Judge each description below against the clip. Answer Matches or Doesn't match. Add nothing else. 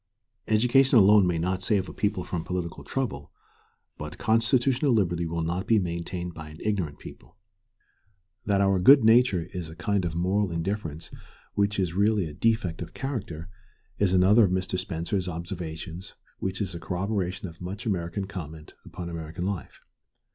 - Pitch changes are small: Doesn't match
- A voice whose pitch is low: Matches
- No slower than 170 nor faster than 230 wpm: Doesn't match